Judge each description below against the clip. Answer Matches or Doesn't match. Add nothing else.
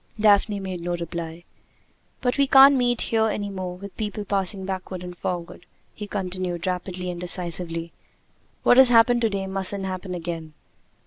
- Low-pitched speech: Doesn't match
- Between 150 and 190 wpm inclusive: Matches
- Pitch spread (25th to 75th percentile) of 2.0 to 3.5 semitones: Matches